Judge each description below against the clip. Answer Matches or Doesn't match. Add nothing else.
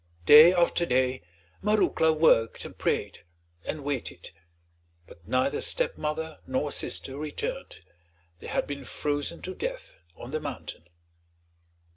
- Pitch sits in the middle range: Matches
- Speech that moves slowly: Matches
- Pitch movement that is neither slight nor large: Matches